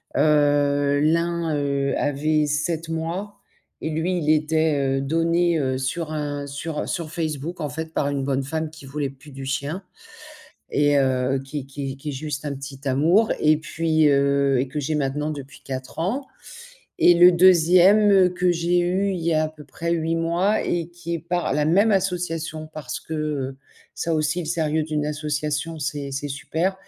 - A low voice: No, medium, 155 Hz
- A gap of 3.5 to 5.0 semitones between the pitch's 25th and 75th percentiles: No, average, 3.0 semitones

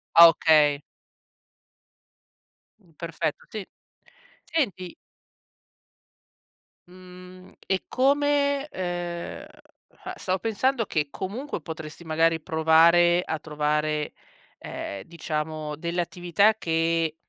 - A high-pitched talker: No, medium, 170 Hz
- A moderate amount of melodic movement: Yes, average, 3.0 semitones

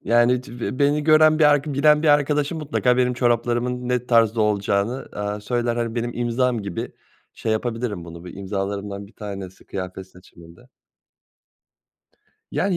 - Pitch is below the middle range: Yes, low, 120 Hz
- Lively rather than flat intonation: No, average, 4.1 semitones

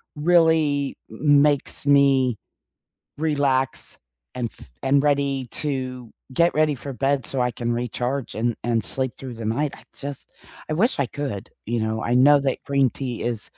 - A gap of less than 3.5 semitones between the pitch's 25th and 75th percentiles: Yes, average, 2.9 semitones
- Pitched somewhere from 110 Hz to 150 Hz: Yes, low, 135 Hz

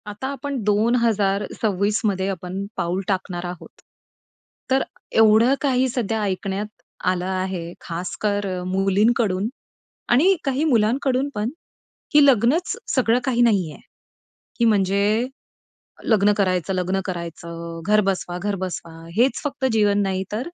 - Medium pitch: No, high, 205 Hz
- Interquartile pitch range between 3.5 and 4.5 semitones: Yes, average, 4.0 semitones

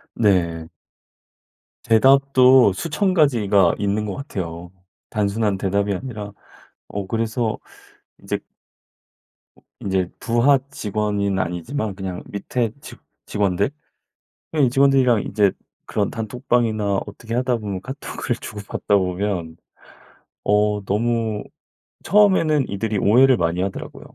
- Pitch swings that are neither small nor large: Yes, average, 4.0 semitones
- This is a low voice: Yes, low, 105 Hz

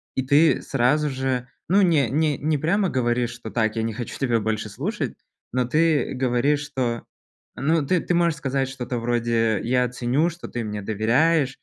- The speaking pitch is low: Yes, low, 130 Hz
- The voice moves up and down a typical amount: Yes, average, 4.2 semitones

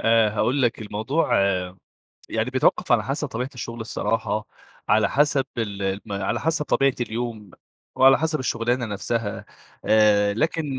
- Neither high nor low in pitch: No, low, 115 Hz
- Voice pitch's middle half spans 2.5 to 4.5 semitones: Yes, average, 3.6 semitones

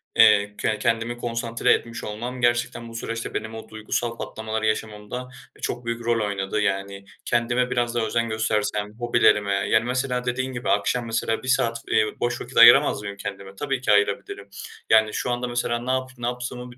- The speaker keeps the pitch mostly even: Yes, narrow, 2.2 semitones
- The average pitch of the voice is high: No, low, 115 Hz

